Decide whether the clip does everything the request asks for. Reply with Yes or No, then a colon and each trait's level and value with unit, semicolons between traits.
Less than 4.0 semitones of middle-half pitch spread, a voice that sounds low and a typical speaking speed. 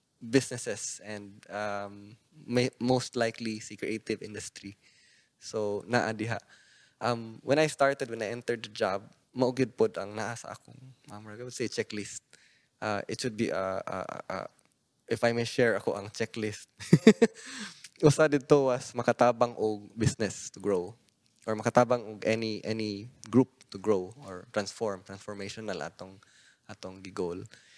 Yes: average, 2.9 semitones; low, 115 Hz; average, 135 wpm